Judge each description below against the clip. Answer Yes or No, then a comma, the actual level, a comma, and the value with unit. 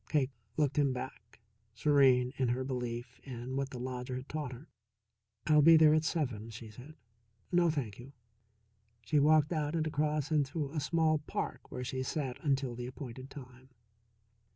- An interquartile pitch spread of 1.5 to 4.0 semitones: Yes, average, 3.2 semitones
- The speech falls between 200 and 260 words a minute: No, average, 170 wpm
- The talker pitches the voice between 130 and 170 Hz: Yes, low, 135 Hz